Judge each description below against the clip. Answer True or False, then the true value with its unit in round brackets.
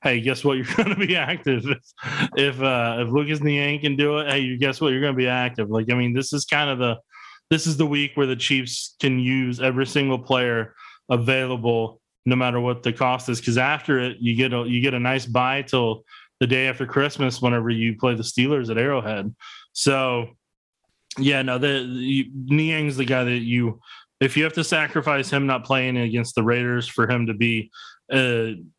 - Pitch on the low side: True (130 Hz)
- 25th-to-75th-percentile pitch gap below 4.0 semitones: True (2.5 semitones)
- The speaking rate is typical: False (210 wpm)